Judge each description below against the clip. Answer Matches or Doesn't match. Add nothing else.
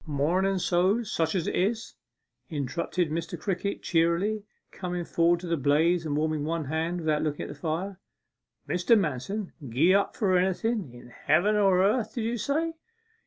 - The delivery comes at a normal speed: Matches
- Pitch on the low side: Doesn't match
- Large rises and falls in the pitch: Doesn't match